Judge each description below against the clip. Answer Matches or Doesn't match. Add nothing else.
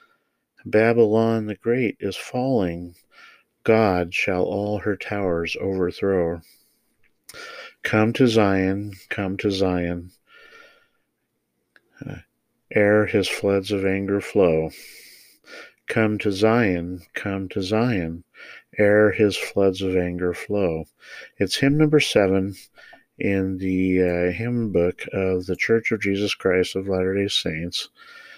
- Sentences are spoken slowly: Matches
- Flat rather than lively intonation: Doesn't match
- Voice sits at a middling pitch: Doesn't match